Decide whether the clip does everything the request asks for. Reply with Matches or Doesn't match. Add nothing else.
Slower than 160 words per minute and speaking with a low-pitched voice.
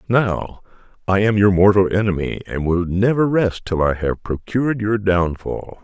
Doesn't match